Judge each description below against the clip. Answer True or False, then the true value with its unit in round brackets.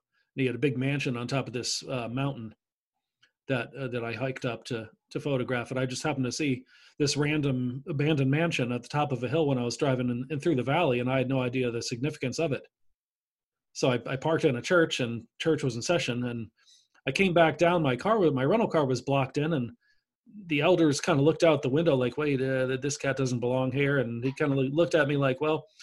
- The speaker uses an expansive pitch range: False (3.5 semitones)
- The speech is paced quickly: True (245 wpm)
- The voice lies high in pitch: False (135 Hz)